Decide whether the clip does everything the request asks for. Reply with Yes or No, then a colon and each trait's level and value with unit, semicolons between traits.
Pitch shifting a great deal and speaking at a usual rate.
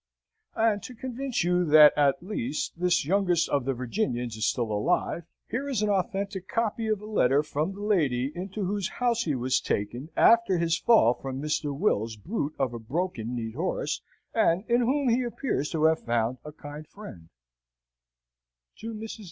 Yes: wide, 8.1 semitones; average, 175 wpm